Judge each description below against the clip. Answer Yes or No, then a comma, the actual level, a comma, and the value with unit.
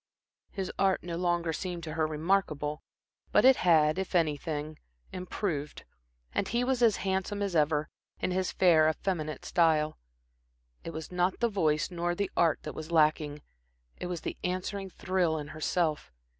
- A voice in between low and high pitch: Yes, medium, 170 Hz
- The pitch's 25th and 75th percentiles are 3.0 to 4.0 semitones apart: Yes, average, 3.3 semitones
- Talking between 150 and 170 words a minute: Yes, average, 160 wpm